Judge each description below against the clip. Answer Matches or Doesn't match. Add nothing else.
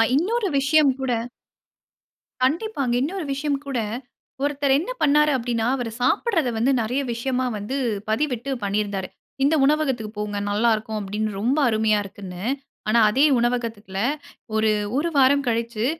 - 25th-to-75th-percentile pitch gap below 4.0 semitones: Doesn't match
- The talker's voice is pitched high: Matches